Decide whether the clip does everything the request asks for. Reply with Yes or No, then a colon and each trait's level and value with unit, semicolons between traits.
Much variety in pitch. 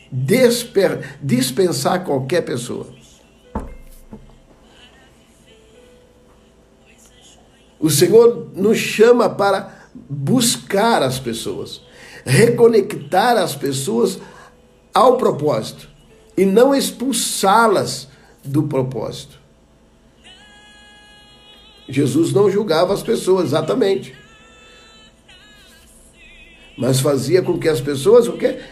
Yes: wide, 6.8 semitones